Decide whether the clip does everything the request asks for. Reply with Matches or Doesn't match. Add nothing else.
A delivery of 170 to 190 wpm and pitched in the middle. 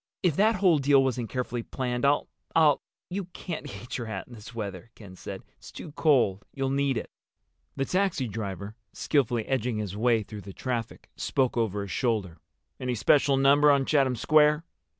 Doesn't match